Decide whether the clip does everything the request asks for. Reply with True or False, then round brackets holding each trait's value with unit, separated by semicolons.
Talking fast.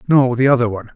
True (250 wpm)